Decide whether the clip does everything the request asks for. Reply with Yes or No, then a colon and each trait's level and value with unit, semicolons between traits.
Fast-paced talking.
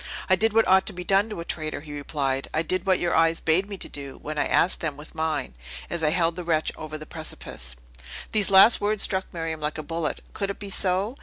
Yes: fast, 245 wpm